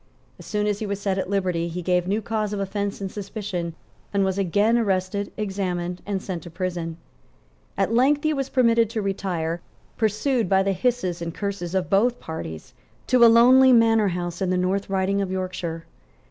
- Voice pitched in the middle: No, high, 195 Hz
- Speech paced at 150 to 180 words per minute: No, average, 190 wpm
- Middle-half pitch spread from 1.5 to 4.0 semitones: Yes, average, 3.1 semitones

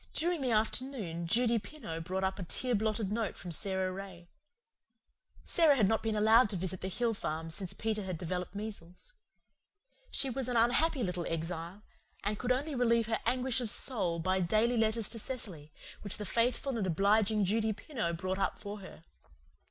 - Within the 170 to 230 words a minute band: Yes, average, 180 wpm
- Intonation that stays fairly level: No, average, 4.1 semitones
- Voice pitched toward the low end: No, high, 210 Hz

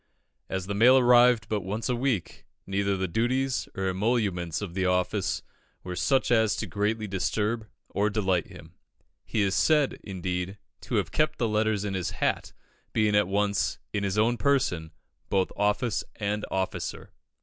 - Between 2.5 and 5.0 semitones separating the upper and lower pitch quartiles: Yes, average, 3.3 semitones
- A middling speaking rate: Yes, average, 165 wpm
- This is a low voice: Yes, low, 105 Hz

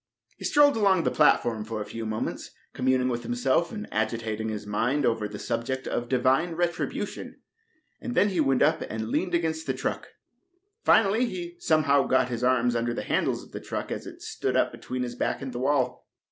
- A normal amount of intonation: No, wide, 6.5 semitones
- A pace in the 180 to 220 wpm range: Yes, average, 195 wpm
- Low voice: Yes, low, 130 Hz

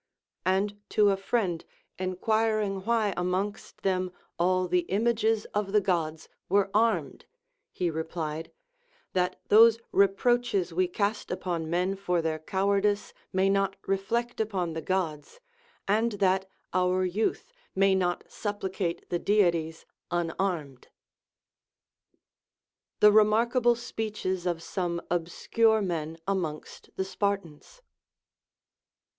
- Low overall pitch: No, high, 190 Hz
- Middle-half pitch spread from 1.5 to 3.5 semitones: Yes, average, 3.0 semitones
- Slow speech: Yes, slow, 115 wpm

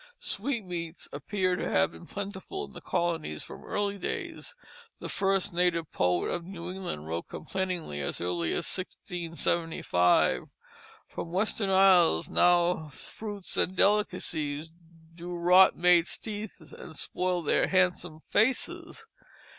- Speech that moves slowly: Yes, slow, 130 wpm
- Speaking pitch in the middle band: Yes, medium, 175 Hz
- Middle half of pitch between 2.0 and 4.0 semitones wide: Yes, average, 3.2 semitones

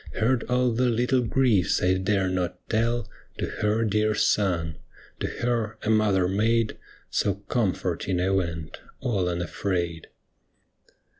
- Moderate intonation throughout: Yes, average, 4.0 semitones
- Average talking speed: No, slow, 130 wpm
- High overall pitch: No, low, 105 Hz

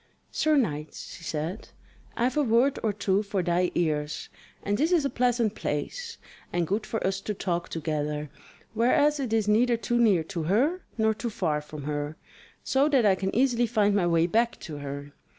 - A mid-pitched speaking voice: No, high, 205 Hz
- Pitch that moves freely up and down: Yes, wide, 6.6 semitones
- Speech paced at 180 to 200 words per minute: Yes, average, 195 wpm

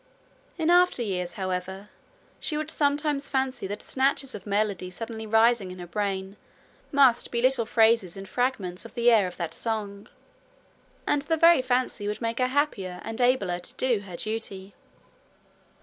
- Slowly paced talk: No, average, 165 wpm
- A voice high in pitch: Yes, high, 225 Hz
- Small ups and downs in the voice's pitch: No, average, 5.1 semitones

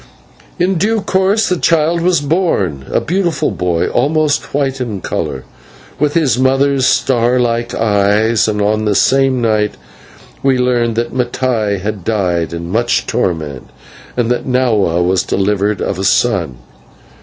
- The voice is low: Yes, low, 120 Hz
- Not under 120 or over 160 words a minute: Yes, average, 145 wpm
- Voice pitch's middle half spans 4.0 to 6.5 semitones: Yes, wide, 5.5 semitones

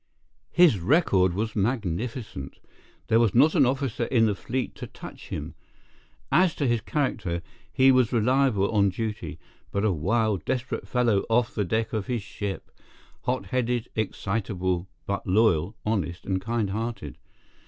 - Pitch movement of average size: Yes, average, 4.0 semitones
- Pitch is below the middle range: Yes, low, 110 Hz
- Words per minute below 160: Yes, average, 145 wpm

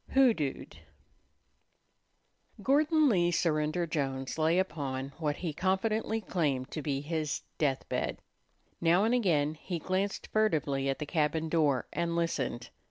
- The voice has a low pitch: No, medium, 160 Hz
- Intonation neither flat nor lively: Yes, average, 4.5 semitones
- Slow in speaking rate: Yes, slow, 130 wpm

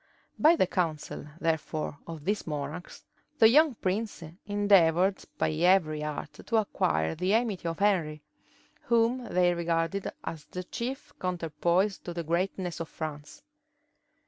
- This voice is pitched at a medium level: Yes, medium, 175 Hz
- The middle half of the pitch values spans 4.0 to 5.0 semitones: Yes, average, 4.3 semitones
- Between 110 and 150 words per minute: Yes, slow, 135 wpm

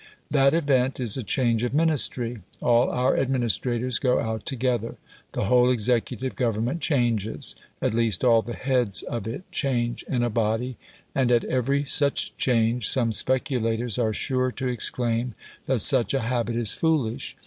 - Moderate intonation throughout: No, narrow, 2.2 semitones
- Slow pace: No, average, 160 wpm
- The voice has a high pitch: No, low, 125 Hz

